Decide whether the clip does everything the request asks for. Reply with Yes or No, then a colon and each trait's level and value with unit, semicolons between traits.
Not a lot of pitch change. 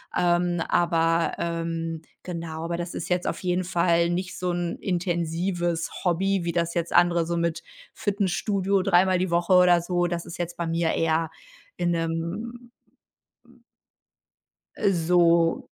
Yes: narrow, 1.2 semitones